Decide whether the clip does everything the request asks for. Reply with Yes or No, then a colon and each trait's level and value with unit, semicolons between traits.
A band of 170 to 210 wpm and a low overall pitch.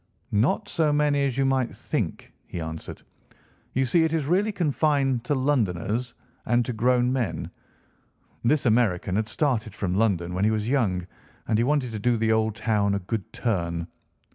Yes: average, 175 wpm; low, 115 Hz